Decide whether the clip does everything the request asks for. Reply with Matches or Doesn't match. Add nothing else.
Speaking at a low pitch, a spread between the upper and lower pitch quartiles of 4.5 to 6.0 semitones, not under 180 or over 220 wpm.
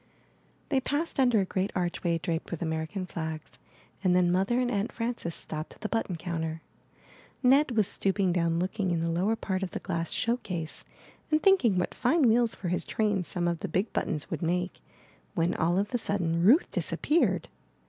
Doesn't match